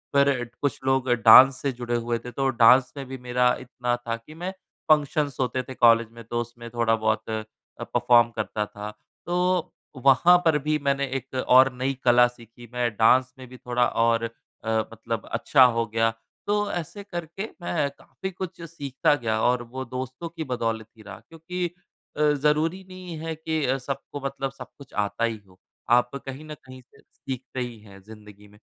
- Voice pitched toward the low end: Yes, low, 125 Hz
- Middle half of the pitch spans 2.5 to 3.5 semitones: No, average, 3.9 semitones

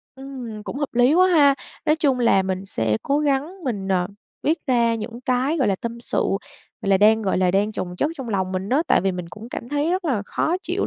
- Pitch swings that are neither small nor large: No, wide, 6.4 semitones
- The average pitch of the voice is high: Yes, high, 235 Hz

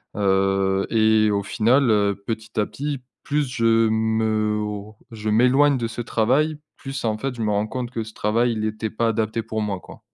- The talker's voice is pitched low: Yes, low, 110 Hz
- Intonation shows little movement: Yes, narrow, 2.0 semitones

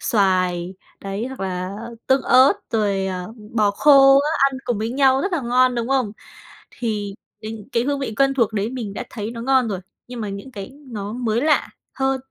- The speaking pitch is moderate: No, high, 230 Hz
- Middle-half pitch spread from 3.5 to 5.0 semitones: Yes, average, 4.7 semitones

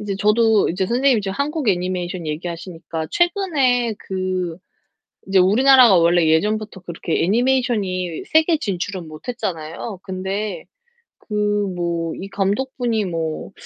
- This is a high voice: Yes, high, 195 Hz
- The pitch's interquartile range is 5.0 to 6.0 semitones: Yes, average, 5.3 semitones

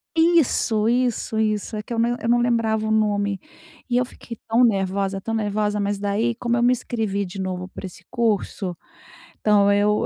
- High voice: Yes, high, 215 Hz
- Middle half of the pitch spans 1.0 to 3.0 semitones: Yes, average, 2.7 semitones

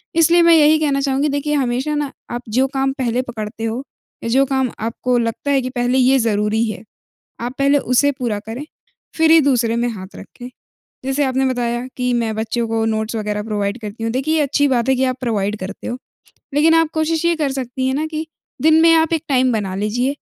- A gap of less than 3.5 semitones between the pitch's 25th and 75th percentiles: No, average, 3.9 semitones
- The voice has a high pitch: Yes, very high, 255 Hz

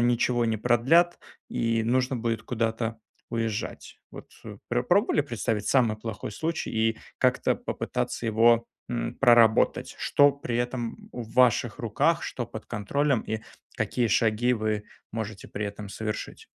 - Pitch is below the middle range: Yes, low, 115 Hz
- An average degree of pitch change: No, narrow, 1.9 semitones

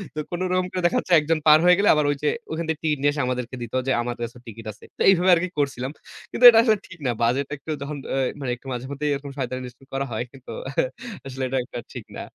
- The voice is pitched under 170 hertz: Yes, medium, 140 Hz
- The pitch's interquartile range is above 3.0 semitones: Yes, average, 4.0 semitones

